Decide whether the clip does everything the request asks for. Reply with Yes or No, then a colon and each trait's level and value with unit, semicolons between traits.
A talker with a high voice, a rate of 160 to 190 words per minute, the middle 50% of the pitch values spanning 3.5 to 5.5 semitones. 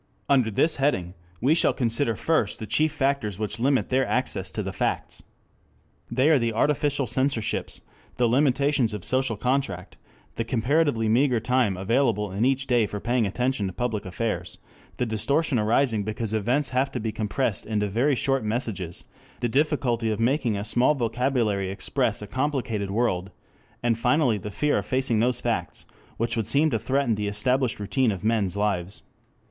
No: low, 120 Hz; average, 170 wpm; average, 4.2 semitones